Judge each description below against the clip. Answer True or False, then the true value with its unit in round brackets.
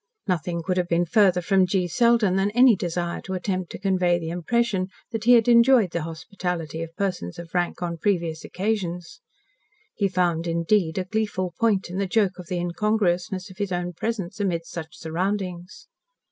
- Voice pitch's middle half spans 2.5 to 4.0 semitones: True (3.0 semitones)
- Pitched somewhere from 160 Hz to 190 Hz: True (185 Hz)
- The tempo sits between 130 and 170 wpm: False (180 wpm)